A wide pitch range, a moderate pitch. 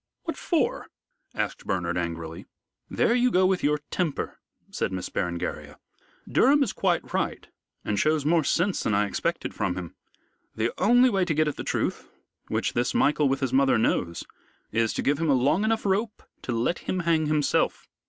Yes: wide, 8.8 semitones; medium, 150 Hz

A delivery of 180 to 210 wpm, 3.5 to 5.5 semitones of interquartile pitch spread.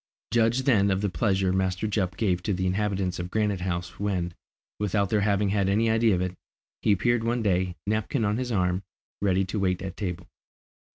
No: average, 195 wpm; average, 2.7 semitones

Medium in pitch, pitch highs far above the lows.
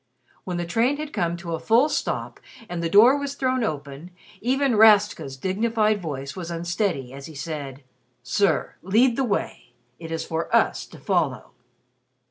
Yes: medium, 180 Hz; wide, 6.3 semitones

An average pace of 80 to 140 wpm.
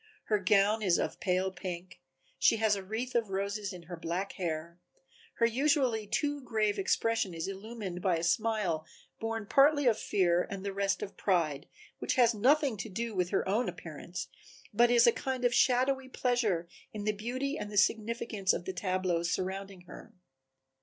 No: average, 180 wpm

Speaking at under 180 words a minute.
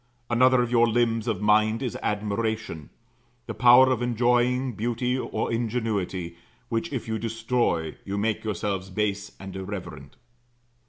Yes: average, 140 wpm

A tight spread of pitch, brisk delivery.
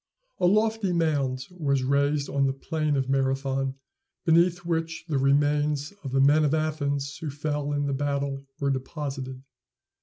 No: narrow, 2.3 semitones; average, 155 wpm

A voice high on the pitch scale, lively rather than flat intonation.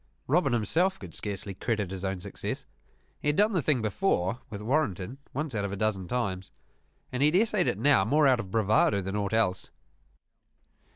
No: low, 110 Hz; wide, 7.1 semitones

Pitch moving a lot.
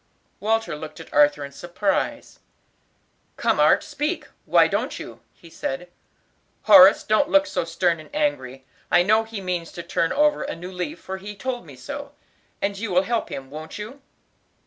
Yes: wide, 6.8 semitones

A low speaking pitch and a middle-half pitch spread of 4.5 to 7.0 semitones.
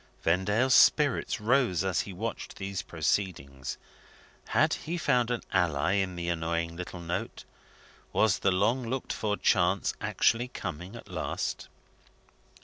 Yes: very low, 95 Hz; average, 5.0 semitones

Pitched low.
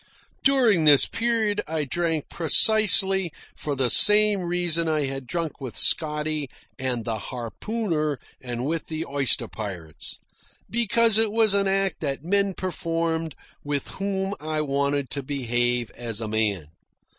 No: medium, 155 Hz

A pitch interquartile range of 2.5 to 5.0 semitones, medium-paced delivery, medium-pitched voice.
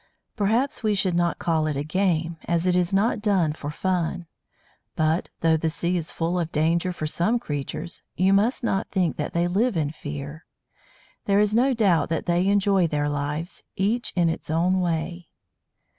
Yes: average, 3.5 semitones; average, 185 wpm; medium, 175 Hz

